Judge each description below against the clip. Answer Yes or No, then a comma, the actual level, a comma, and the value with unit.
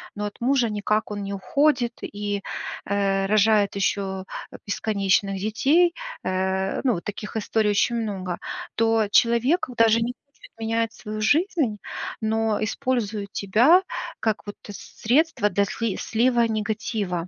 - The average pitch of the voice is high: Yes, high, 215 Hz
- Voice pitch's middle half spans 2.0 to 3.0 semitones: Yes, narrow, 2.6 semitones